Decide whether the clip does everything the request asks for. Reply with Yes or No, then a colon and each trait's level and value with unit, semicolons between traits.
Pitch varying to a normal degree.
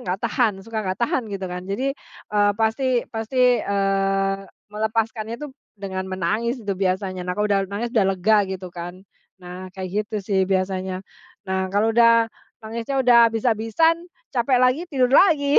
Yes: average, 3.7 semitones